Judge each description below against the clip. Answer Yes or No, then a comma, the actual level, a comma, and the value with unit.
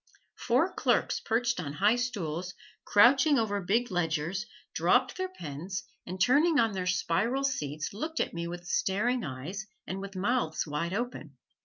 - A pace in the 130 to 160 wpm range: Yes, average, 155 wpm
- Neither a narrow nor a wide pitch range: No, wide, 6.2 semitones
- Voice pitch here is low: No, high, 195 Hz